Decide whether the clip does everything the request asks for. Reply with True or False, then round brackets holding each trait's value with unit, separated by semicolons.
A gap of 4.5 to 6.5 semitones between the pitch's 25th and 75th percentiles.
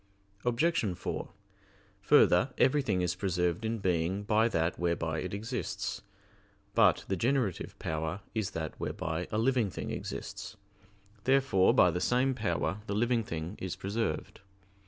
True (5.1 semitones)